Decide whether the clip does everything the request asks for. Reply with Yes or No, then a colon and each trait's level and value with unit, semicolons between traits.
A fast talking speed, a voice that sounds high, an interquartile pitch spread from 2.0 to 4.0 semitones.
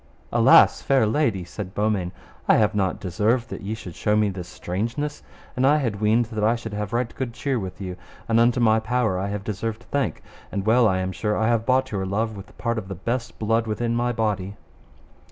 No: fast, 220 wpm; low, 110 Hz; average, 2.9 semitones